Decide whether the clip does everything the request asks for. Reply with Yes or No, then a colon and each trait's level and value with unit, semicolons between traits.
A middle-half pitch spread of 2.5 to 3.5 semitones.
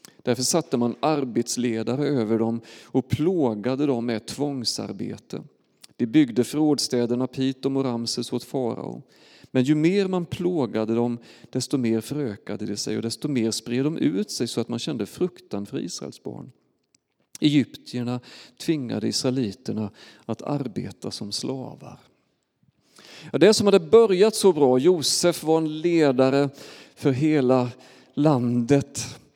No: average, 3.9 semitones